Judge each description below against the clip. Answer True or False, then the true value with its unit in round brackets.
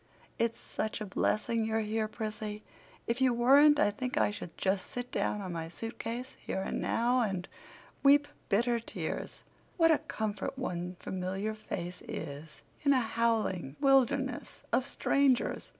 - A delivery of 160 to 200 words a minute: False (150 wpm)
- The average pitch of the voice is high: True (225 Hz)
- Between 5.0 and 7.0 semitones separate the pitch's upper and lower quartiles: False (4.6 semitones)